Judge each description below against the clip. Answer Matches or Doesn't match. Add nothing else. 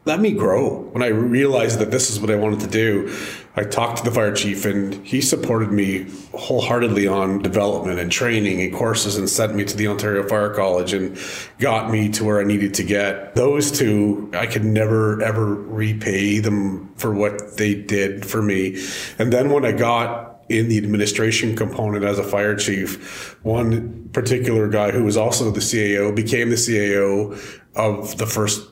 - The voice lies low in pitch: Matches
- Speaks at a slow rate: Doesn't match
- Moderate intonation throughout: Doesn't match